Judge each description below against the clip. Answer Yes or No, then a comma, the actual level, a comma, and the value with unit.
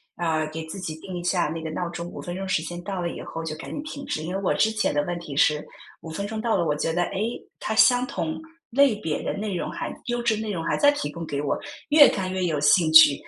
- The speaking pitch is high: No, medium, 175 Hz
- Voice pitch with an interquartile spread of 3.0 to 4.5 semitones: No, average, 4.9 semitones